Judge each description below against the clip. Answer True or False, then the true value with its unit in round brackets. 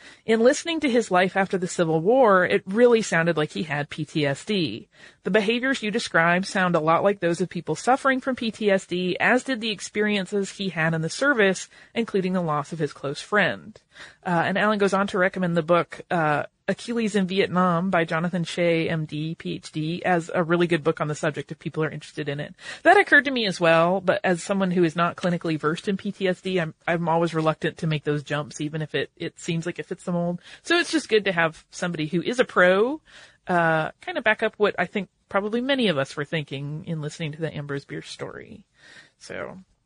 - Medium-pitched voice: True (180 Hz)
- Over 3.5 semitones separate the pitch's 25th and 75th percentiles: True (3.9 semitones)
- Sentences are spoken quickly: True (220 wpm)